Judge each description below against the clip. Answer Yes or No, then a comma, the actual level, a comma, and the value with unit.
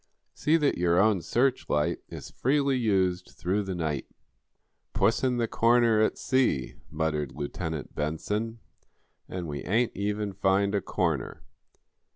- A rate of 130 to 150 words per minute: Yes, average, 140 wpm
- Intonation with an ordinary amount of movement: No, wide, 6.1 semitones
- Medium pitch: No, low, 100 Hz